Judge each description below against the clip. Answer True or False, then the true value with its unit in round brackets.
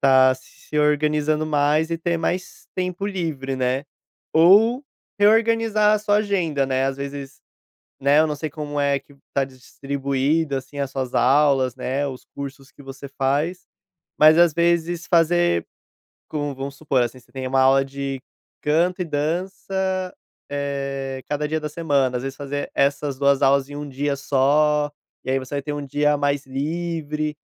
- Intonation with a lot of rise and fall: False (3.0 semitones)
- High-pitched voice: False (145 Hz)